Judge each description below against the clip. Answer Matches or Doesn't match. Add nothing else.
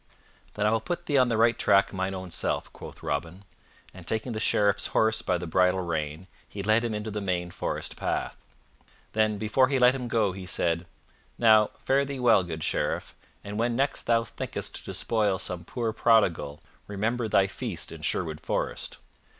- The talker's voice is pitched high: Doesn't match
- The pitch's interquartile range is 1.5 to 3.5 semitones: Doesn't match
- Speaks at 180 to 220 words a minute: Matches